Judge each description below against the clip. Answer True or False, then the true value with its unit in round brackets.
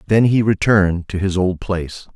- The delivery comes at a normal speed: True (195 wpm)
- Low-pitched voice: True (95 Hz)